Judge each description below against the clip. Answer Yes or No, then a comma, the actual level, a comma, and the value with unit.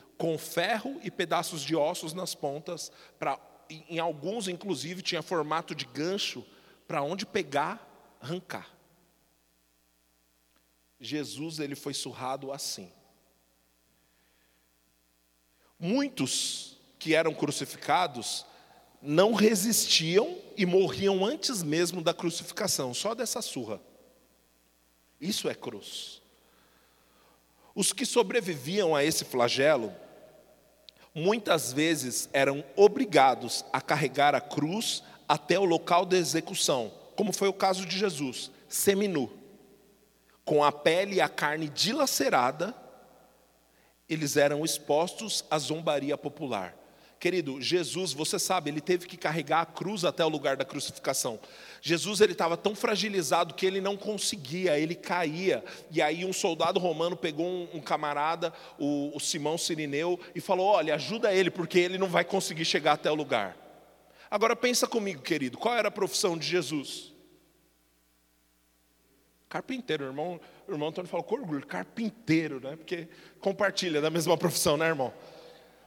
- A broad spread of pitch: No, average, 4.9 semitones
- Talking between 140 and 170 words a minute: No, average, 125 wpm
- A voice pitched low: No, medium, 165 Hz